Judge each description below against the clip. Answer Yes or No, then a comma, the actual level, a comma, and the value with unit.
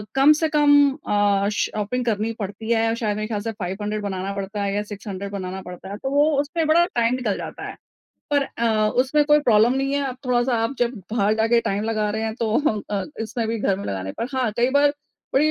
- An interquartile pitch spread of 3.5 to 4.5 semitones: Yes, average, 4.2 semitones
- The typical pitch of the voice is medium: No, high, 225 Hz